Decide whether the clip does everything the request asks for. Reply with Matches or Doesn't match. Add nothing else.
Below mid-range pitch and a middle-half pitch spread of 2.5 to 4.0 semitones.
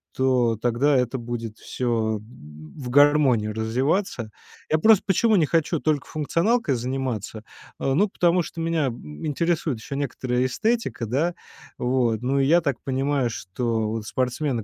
Doesn't match